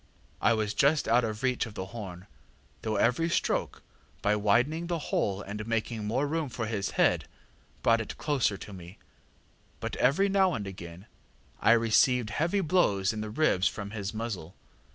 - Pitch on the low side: Yes, low, 110 Hz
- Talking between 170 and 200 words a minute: Yes, average, 175 wpm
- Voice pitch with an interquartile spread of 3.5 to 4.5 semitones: No, average, 5.2 semitones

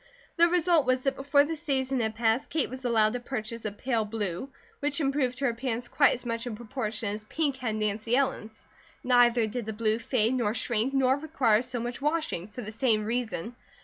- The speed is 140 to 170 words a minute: No, fast, 205 wpm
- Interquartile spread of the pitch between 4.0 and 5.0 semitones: No, average, 3.5 semitones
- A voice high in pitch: Yes, high, 245 Hz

